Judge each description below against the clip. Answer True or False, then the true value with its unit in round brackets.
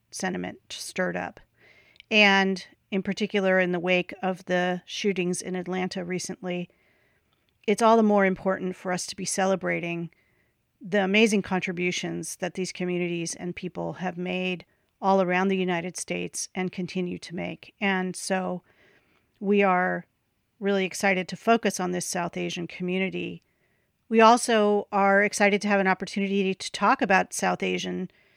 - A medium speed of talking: True (150 wpm)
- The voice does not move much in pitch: True (1.7 semitones)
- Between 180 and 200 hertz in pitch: True (185 Hz)